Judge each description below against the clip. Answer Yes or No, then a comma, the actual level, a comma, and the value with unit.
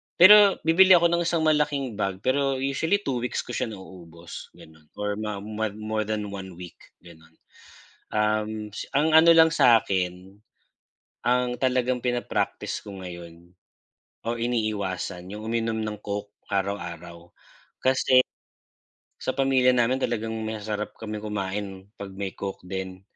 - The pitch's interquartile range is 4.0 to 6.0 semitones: Yes, average, 5.0 semitones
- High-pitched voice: No, low, 110 Hz